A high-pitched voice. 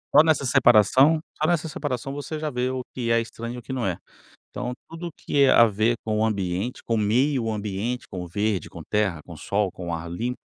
No: low, 115 Hz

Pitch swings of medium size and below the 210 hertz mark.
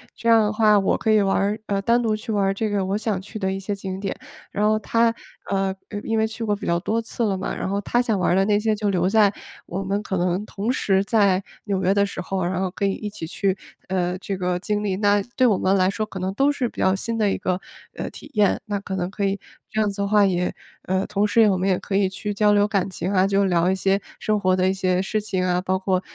No: narrow, 2.0 semitones; high, 200 Hz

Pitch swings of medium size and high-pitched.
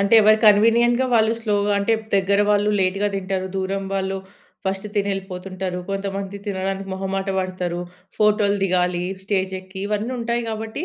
No: narrow, 1.8 semitones; high, 195 Hz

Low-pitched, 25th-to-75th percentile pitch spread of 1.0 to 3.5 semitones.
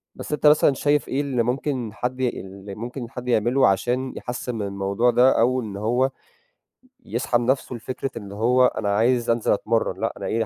Yes: low, 120 Hz; average, 2.8 semitones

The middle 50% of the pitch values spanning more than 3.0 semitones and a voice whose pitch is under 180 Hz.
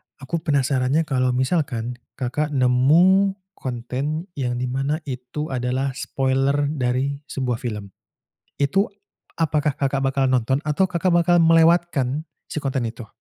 Yes: average, 3.5 semitones; low, 135 Hz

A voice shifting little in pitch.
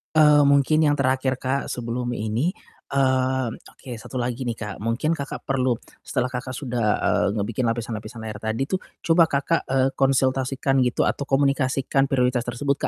Yes: narrow, 2.3 semitones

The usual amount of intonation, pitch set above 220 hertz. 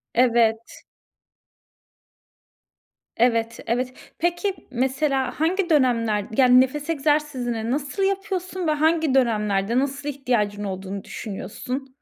Yes: average, 4.8 semitones; very high, 260 Hz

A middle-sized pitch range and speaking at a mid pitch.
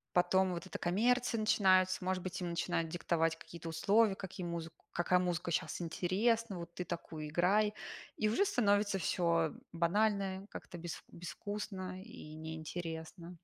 Yes: average, 3.1 semitones; medium, 180 Hz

